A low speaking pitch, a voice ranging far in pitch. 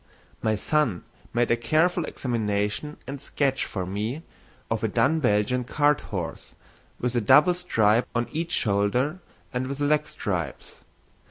Yes: low, 125 Hz; wide, 5.7 semitones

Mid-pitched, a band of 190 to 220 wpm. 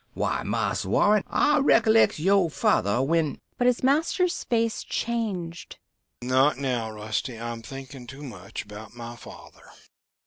No: medium, 145 Hz; slow, 135 wpm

